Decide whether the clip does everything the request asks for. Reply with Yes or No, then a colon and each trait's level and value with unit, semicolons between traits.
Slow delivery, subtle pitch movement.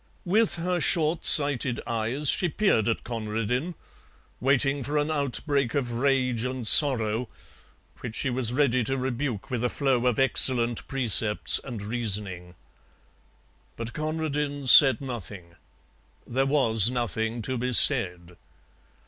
No: slow, 130 wpm; average, 3.8 semitones